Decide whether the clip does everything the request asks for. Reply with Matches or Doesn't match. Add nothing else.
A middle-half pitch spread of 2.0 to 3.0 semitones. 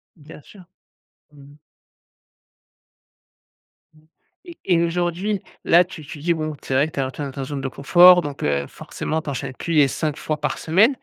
Doesn't match